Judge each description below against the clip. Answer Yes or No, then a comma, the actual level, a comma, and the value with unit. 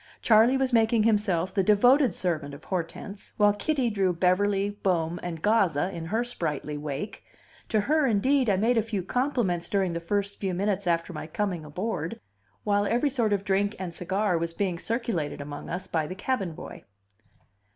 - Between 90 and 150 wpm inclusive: No, average, 180 wpm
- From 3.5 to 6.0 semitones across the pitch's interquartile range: Yes, average, 4.4 semitones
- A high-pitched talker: Yes, high, 195 Hz